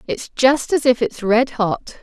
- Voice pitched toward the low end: No, high, 240 Hz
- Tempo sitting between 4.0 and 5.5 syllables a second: Yes, 4.4 syllables/s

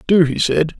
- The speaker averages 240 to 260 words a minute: No, fast, 225 wpm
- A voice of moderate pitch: Yes, medium, 165 Hz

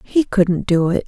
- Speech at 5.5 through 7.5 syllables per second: No, 4.2 syllables/s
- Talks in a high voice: Yes, high, 195 Hz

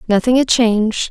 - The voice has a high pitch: Yes, high, 230 Hz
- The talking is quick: No, average, 165 wpm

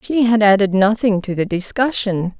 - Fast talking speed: No, average, 175 wpm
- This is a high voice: Yes, high, 210 Hz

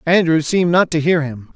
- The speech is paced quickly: Yes, fast, 230 wpm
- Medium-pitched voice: Yes, medium, 160 Hz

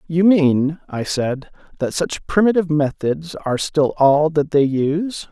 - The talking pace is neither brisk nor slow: Yes, average, 160 wpm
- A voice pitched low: No, medium, 155 Hz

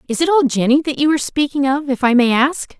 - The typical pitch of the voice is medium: No, very high, 275 Hz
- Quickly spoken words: Yes, fast, 280 wpm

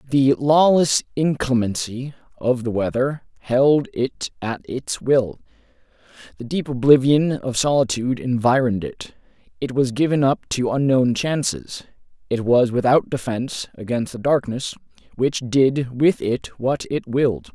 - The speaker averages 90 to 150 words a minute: Yes, slow, 135 wpm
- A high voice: No, low, 125 Hz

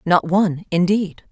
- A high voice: No, medium, 180 Hz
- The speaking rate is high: No, slow, 135 wpm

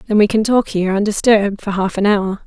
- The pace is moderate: No, fast, 245 wpm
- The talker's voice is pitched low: No, high, 205 Hz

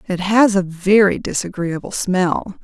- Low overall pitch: No, high, 190 Hz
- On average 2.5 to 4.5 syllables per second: Yes, 4.1 syllables/s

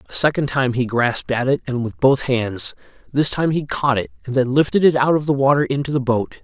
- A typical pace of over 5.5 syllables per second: Yes, 5.7 syllables/s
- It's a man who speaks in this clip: Yes, male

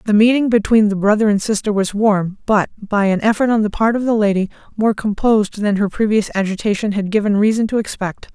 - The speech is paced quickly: Yes, fast, 215 wpm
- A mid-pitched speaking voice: No, high, 210 Hz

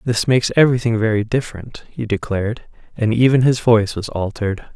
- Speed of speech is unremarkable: Yes, average, 165 wpm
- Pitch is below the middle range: Yes, low, 115 Hz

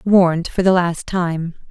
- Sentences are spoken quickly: No, average, 175 wpm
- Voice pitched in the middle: Yes, medium, 175 Hz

